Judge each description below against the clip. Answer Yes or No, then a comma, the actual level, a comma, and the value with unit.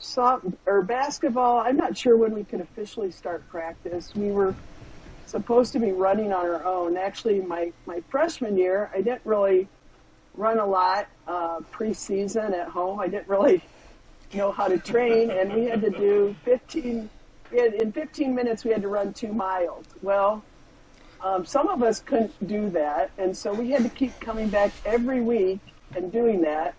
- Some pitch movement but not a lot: Yes, average, 4.0 semitones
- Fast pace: No, average, 180 wpm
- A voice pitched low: No, high, 205 Hz